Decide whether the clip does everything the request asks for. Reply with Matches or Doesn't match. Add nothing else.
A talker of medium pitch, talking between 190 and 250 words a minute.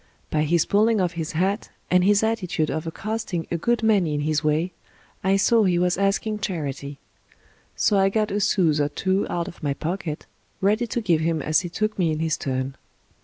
Matches